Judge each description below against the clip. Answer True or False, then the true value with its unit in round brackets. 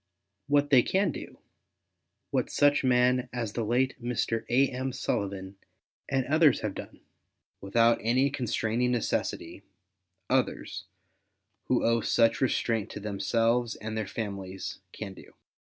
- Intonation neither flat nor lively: True (3.0 semitones)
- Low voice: True (120 Hz)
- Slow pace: True (130 wpm)